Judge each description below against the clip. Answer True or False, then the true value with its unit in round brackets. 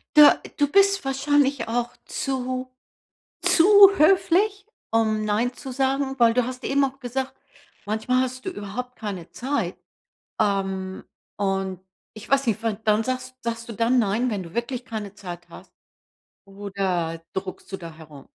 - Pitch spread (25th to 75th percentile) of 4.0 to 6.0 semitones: True (4.9 semitones)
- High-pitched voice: True (235 Hz)